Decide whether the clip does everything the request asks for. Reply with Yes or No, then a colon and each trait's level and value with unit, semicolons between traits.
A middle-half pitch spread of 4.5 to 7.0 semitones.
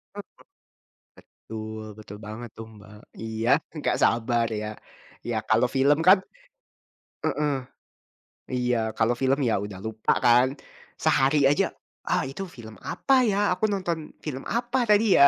Yes: average, 5.1 semitones